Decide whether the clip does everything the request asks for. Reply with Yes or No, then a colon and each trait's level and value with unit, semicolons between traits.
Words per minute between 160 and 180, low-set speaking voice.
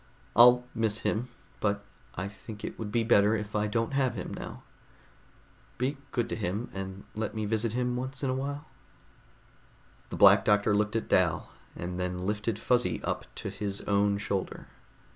Yes: average, 175 wpm; low, 105 Hz